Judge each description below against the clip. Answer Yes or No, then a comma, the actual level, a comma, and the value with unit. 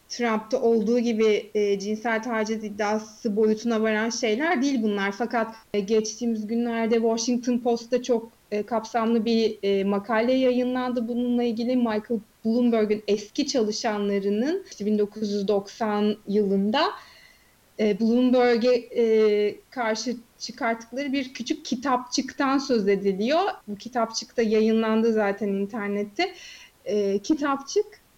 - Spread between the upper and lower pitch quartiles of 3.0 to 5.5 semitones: No, narrow, 2.5 semitones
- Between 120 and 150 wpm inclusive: No, average, 110 wpm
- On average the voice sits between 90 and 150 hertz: No, high, 230 Hz